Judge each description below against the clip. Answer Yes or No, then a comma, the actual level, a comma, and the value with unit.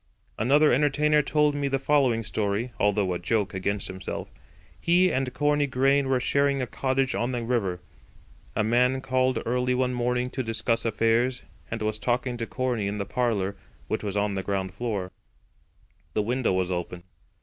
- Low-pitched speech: Yes, low, 120 Hz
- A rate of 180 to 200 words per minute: No, average, 170 wpm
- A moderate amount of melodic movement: Yes, average, 4.3 semitones